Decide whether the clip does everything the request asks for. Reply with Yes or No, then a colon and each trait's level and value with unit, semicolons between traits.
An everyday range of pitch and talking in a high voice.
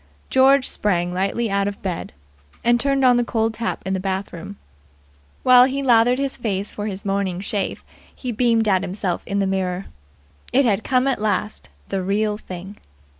Yes: average, 4.0 semitones; high, 210 Hz